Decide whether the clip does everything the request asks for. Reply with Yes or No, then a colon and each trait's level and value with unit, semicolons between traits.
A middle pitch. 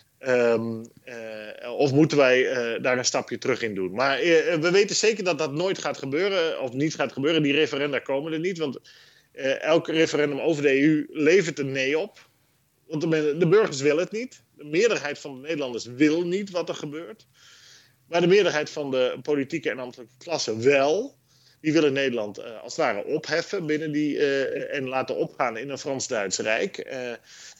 Yes: medium, 150 Hz